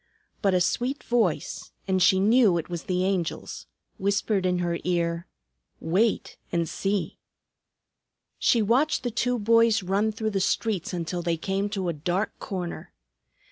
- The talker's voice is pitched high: Yes, high, 195 Hz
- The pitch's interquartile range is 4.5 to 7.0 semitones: No, average, 3.7 semitones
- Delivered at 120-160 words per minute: Yes, average, 150 wpm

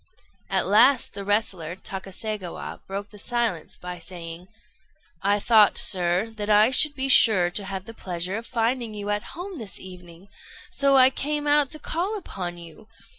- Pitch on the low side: No, high, 205 Hz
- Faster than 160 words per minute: Yes, average, 170 wpm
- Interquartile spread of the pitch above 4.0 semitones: Yes, average, 5.2 semitones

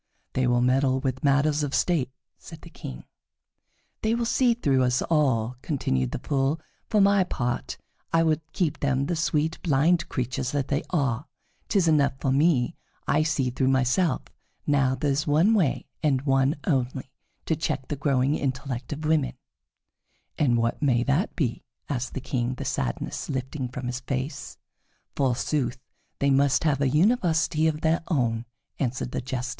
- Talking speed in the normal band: Yes, average, 170 wpm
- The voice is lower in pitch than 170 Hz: Yes, medium, 140 Hz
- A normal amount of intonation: Yes, average, 3.4 semitones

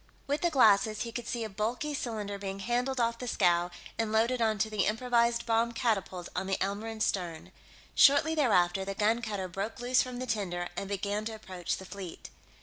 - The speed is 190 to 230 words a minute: Yes, average, 195 wpm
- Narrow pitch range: No, average, 3.4 semitones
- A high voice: Yes, high, 220 Hz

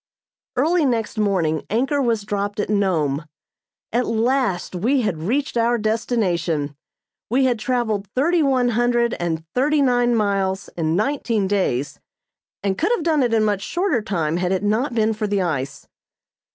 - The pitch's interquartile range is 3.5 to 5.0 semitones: Yes, average, 4.7 semitones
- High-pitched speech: Yes, high, 215 Hz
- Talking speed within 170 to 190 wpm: No, average, 160 wpm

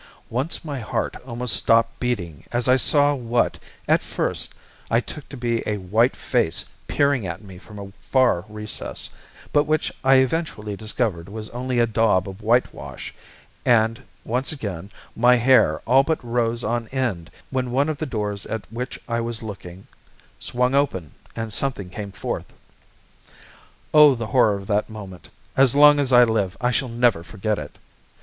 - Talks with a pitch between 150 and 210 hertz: No, low, 115 Hz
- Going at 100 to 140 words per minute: No, average, 170 wpm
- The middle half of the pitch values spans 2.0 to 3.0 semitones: No, average, 3.7 semitones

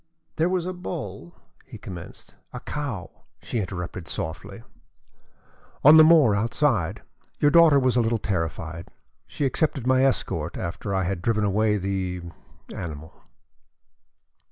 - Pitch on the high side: No, low, 105 Hz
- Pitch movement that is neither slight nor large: No, wide, 7.6 semitones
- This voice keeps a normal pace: No, slow, 130 wpm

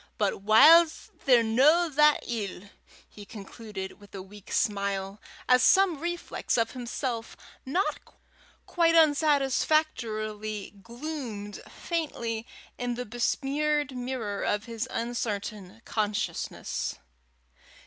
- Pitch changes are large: Yes, wide, 5.9 semitones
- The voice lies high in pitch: Yes, high, 235 Hz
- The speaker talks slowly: Yes, slow, 100 wpm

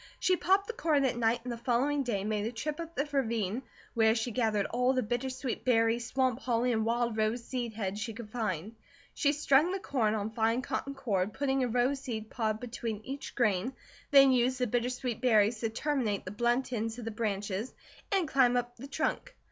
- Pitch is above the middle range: Yes, high, 240 Hz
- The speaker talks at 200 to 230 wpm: Yes, fast, 205 wpm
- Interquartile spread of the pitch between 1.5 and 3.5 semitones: Yes, average, 3.2 semitones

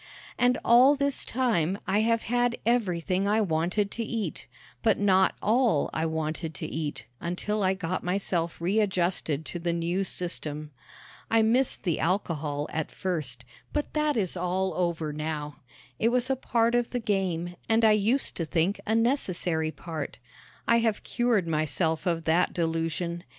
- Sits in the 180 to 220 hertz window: Yes, medium, 185 Hz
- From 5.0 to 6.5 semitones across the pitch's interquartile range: Yes, wide, 5.6 semitones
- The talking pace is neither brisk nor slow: Yes, average, 160 wpm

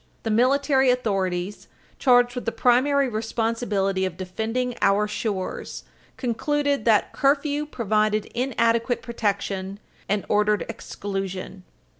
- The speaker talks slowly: Yes, slow, 105 wpm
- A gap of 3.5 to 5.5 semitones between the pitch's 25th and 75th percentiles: Yes, average, 3.9 semitones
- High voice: Yes, high, 225 Hz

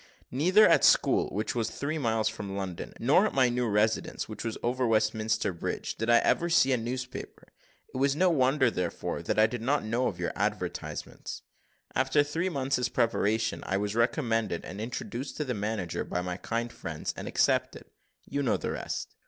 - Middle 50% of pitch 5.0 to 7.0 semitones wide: No, average, 3.5 semitones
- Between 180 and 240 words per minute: Yes, average, 190 wpm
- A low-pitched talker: Yes, low, 115 Hz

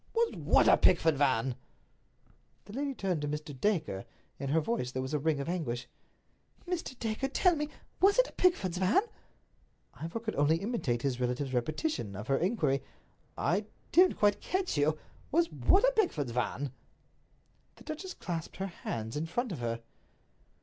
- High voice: No, medium, 165 Hz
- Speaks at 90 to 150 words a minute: No, average, 165 wpm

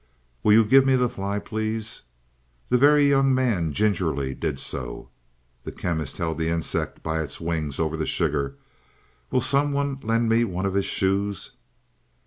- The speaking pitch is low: Yes, low, 100 Hz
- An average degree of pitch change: No, wide, 7.5 semitones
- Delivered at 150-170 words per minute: Yes, average, 160 wpm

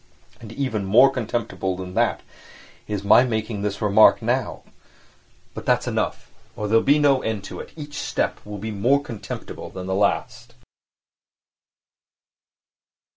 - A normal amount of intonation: Yes, average, 4.1 semitones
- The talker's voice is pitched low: Yes, low, 110 Hz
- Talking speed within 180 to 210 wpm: No, average, 145 wpm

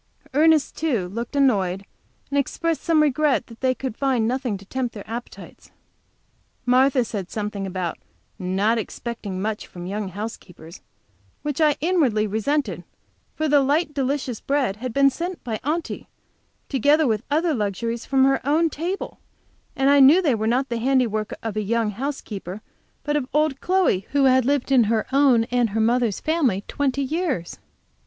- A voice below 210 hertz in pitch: No, very high, 255 Hz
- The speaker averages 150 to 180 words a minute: Yes, average, 165 wpm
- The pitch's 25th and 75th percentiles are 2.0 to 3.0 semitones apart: No, average, 5.0 semitones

